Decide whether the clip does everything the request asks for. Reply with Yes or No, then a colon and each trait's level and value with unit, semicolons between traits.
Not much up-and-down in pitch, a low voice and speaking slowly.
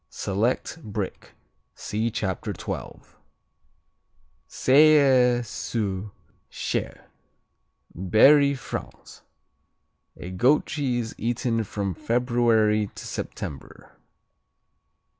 No: average, 3.6 semitones; low, 115 Hz; slow, 70 wpm